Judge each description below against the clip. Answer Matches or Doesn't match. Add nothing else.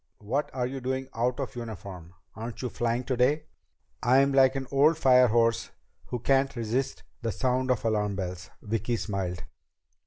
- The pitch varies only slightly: Doesn't match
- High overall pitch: Doesn't match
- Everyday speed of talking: Matches